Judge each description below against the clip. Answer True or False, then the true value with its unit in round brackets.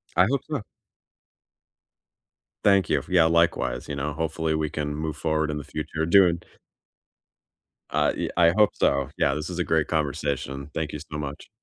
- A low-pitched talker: True (80 Hz)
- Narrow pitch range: True (2.3 semitones)